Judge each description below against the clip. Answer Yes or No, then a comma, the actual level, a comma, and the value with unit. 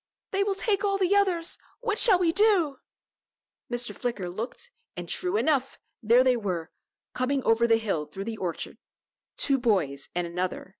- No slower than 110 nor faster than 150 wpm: No, average, 165 wpm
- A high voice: Yes, very high, 250 Hz